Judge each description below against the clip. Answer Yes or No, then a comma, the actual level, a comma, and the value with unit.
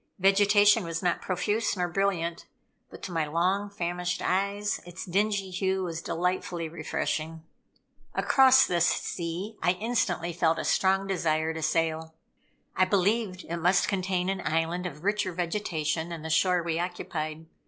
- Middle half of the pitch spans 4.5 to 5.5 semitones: No, average, 2.9 semitones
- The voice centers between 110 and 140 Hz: No, medium, 180 Hz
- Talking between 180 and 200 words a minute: No, average, 150 wpm